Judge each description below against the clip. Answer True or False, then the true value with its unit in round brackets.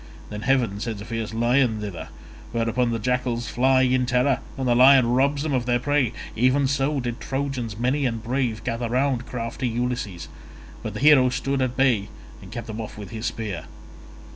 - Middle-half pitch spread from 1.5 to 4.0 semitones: True (2.5 semitones)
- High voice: False (125 Hz)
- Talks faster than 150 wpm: True (185 wpm)